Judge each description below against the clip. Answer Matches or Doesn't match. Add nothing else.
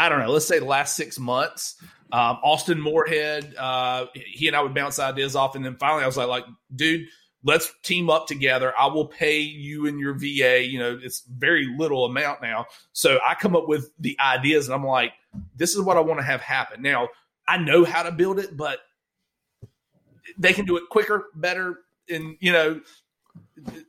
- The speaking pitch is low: Doesn't match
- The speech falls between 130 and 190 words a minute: Doesn't match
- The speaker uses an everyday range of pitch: Matches